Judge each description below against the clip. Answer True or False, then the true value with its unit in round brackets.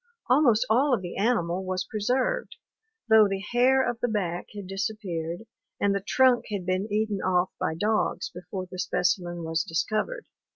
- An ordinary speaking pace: True (165 wpm)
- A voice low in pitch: False (200 Hz)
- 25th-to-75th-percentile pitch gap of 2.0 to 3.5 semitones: False (4.4 semitones)